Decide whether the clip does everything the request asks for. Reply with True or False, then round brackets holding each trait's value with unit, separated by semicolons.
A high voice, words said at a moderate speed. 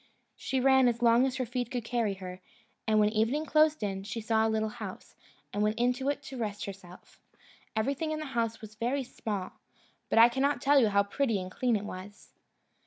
False (230 Hz; 210 wpm)